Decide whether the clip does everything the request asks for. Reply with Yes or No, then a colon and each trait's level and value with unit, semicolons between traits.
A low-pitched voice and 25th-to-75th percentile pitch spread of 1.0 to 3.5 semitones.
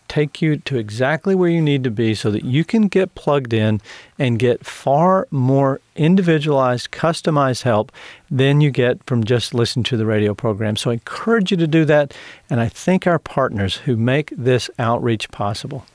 No: low, 130 Hz; average, 4.9 semitones